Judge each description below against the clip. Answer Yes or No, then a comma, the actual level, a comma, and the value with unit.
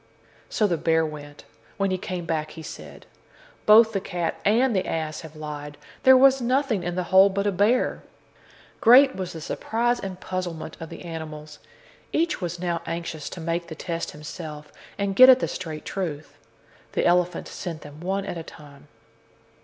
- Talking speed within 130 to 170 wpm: No, average, 180 wpm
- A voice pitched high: No, medium, 175 Hz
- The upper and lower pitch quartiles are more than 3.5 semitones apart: Yes, average, 4.1 semitones